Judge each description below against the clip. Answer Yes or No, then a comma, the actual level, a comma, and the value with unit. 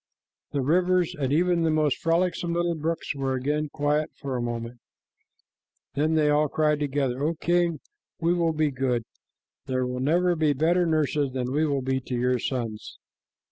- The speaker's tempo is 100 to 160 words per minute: No, average, 170 wpm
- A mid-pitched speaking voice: Yes, medium, 150 Hz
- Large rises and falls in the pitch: No, average, 3.9 semitones